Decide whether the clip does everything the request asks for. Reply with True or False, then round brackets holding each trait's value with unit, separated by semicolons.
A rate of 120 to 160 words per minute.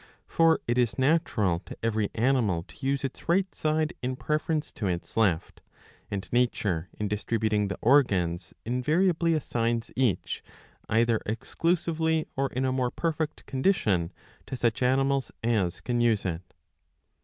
True (150 wpm)